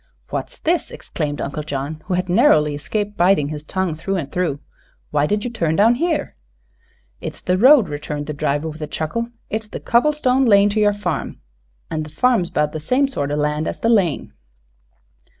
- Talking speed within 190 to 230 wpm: Yes, average, 195 wpm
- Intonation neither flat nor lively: No, wide, 6.7 semitones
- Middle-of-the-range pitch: Yes, medium, 180 Hz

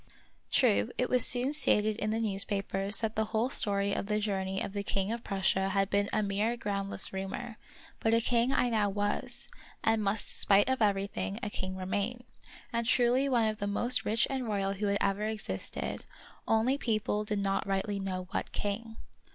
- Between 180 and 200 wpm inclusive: Yes, average, 190 wpm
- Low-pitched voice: No, high, 210 Hz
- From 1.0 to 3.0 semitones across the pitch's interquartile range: Yes, narrow, 2.5 semitones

